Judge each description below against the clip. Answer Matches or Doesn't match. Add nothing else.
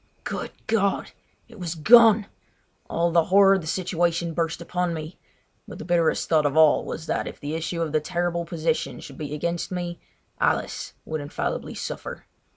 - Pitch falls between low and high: Matches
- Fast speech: Doesn't match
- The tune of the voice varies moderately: Doesn't match